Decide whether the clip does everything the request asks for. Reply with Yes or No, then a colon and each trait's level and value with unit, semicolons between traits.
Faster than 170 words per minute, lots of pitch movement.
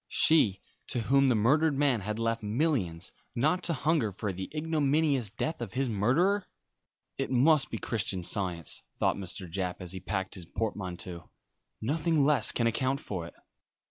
No: average, 165 wpm; wide, 7.3 semitones